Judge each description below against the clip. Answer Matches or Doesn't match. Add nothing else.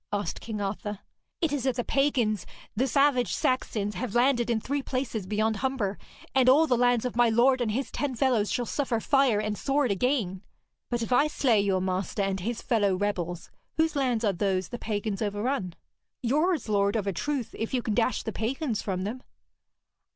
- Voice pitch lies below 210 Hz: Doesn't match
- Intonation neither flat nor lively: Matches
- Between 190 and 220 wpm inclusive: Matches